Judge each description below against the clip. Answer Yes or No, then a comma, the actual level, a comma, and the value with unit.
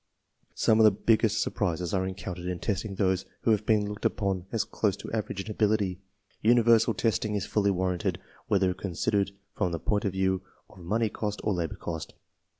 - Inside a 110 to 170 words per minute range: No, average, 185 wpm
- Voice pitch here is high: No, low, 100 Hz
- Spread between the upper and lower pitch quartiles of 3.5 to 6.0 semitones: No, average, 2.7 semitones